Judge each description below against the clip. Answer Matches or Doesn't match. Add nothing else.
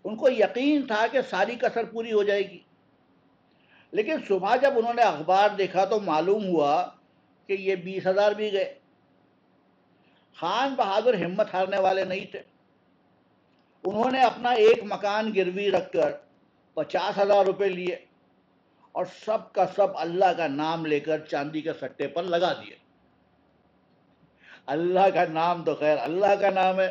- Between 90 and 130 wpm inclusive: Doesn't match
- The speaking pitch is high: Matches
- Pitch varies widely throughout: Doesn't match